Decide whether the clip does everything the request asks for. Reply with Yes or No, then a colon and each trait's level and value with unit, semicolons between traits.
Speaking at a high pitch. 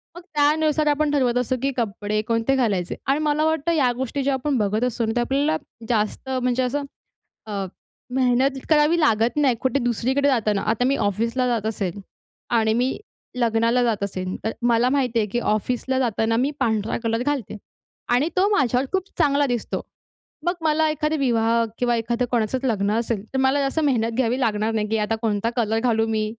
Yes: high, 245 Hz